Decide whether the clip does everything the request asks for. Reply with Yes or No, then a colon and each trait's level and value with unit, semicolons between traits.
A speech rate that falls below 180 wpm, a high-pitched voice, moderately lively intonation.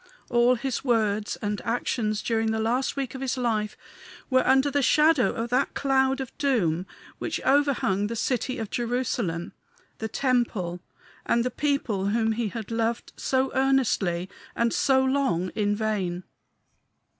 Yes: average, 150 wpm; high, 235 Hz; average, 3.8 semitones